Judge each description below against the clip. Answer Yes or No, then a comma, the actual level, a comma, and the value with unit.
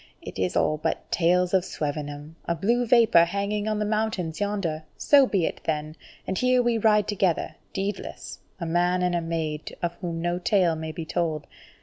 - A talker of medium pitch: Yes, medium, 175 Hz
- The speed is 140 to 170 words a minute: No, average, 190 wpm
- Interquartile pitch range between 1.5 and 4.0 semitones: No, average, 4.4 semitones